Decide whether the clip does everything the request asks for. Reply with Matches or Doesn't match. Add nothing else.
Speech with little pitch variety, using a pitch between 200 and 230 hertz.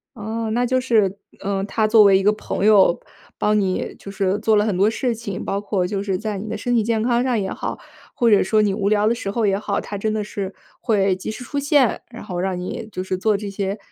Matches